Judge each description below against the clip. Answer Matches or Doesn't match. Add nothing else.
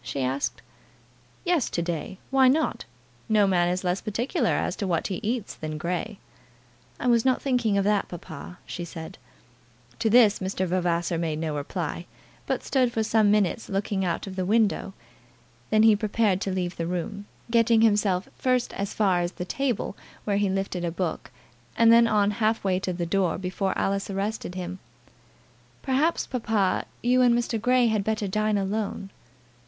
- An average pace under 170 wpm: Doesn't match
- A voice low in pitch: Doesn't match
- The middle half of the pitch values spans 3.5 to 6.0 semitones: Matches